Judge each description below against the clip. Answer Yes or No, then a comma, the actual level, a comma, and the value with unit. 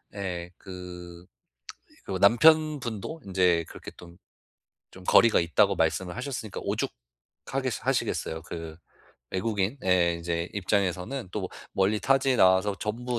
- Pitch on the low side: Yes, very low, 95 Hz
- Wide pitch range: No, average, 4.5 semitones